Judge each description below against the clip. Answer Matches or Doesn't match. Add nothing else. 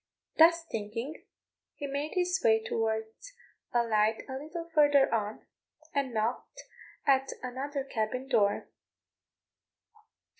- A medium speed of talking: Doesn't match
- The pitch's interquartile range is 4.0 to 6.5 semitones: Matches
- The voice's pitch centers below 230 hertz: Doesn't match